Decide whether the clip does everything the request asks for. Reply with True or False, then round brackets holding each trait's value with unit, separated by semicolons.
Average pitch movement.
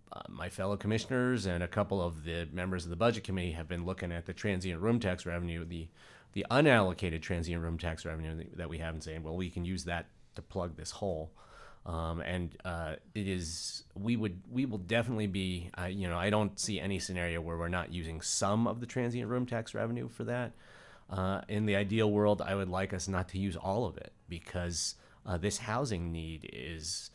True (3.5 semitones)